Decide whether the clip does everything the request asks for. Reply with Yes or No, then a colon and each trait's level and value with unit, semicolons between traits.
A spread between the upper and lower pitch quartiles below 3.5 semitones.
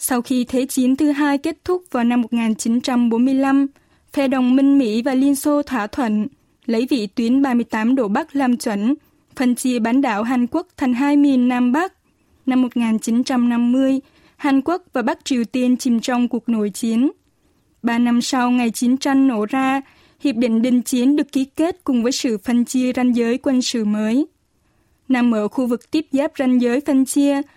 Yes: narrow, 2.5 semitones